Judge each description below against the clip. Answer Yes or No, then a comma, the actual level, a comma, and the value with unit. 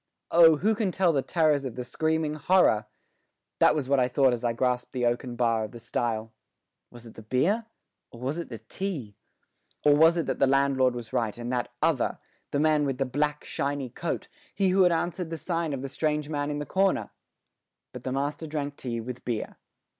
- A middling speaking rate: No, fast, 215 wpm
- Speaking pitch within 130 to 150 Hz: Yes, medium, 140 Hz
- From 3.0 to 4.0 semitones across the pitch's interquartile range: No, average, 4.4 semitones